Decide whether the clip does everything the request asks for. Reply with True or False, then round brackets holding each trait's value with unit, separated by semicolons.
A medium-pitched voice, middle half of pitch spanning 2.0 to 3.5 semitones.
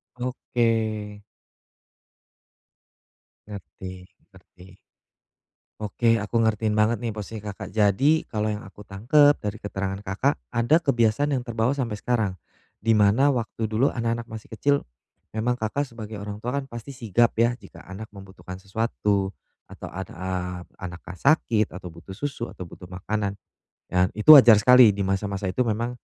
False (110 Hz; 3.2 semitones)